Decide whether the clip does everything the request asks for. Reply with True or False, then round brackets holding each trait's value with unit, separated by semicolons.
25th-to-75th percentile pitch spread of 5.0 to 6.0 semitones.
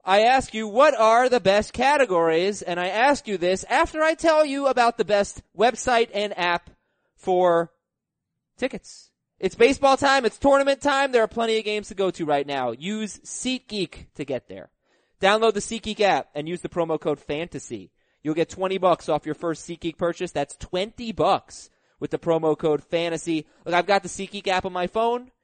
True (5.6 semitones)